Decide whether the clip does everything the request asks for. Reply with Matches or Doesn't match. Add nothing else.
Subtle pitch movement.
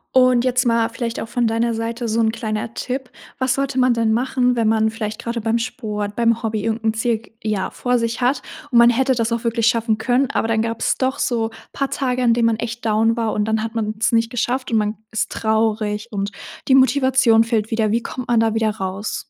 Matches